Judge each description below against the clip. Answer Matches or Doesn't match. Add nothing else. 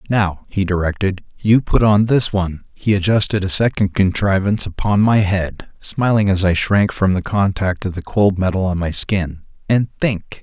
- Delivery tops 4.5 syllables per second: Matches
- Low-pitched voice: Matches